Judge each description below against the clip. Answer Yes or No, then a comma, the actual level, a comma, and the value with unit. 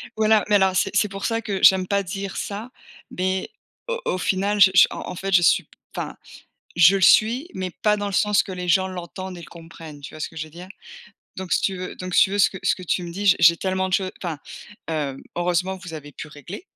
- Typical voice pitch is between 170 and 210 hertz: Yes, medium, 185 Hz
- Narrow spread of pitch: Yes, narrow, 2.3 semitones